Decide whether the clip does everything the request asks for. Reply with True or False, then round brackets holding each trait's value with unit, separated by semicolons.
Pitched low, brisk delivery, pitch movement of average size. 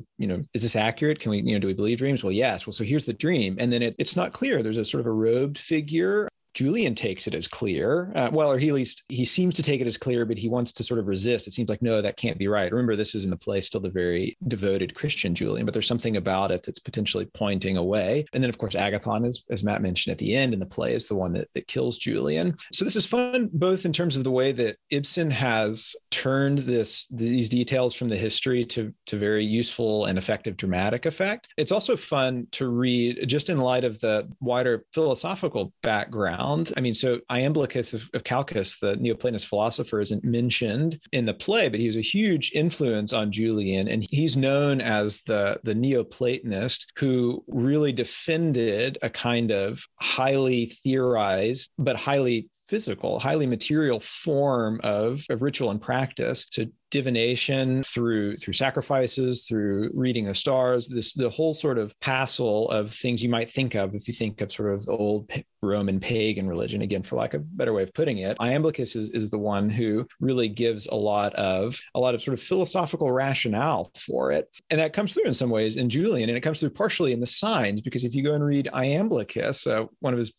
True (120 Hz; 215 wpm; 4.1 semitones)